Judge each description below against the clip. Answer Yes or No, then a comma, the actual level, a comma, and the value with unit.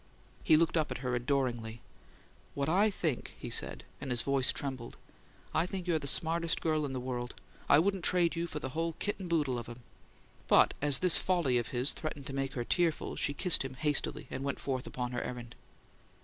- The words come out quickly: Yes, fast, 210 wpm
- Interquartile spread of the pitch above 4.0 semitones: Yes, average, 4.6 semitones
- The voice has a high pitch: No, medium, 140 Hz